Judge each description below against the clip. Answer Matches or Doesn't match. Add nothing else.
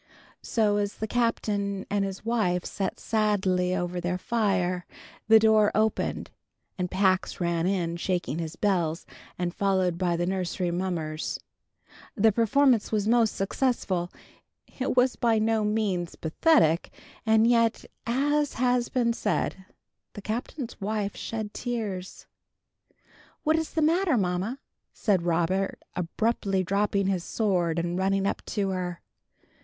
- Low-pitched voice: Doesn't match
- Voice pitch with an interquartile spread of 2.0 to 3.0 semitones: Doesn't match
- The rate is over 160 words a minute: Doesn't match